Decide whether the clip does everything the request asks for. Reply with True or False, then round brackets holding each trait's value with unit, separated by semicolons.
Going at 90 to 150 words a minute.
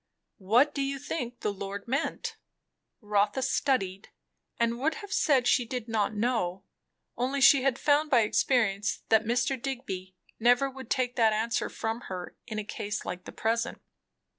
False (165 wpm)